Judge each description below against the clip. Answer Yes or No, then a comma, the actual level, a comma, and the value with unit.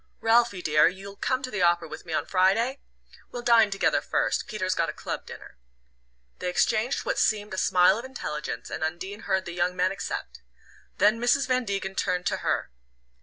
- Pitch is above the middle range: Yes, high, 195 Hz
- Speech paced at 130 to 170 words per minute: No, average, 190 wpm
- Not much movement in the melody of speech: No, average, 4.3 semitones